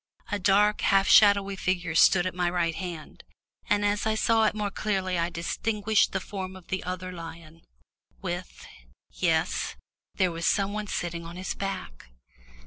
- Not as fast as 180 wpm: Yes, average, 165 wpm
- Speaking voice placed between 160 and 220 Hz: Yes, medium, 185 Hz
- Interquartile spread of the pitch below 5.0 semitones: Yes, average, 2.9 semitones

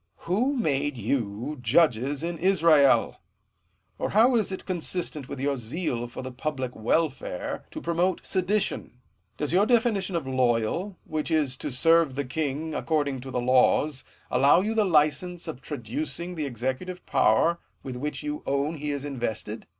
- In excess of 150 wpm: Yes, average, 160 wpm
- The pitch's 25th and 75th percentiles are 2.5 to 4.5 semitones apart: No, average, 5.2 semitones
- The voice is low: No, medium, 150 Hz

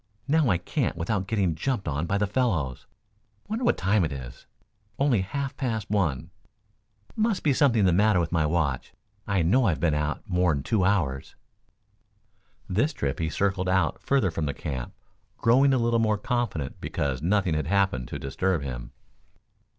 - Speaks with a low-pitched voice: Yes, very low, 95 Hz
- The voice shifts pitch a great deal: Yes, wide, 6.7 semitones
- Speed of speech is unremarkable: Yes, average, 170 wpm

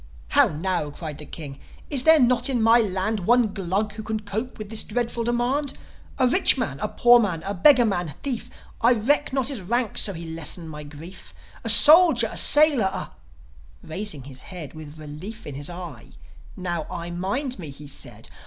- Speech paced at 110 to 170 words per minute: No, average, 195 wpm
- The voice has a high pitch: Yes, high, 200 Hz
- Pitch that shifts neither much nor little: No, wide, 6.9 semitones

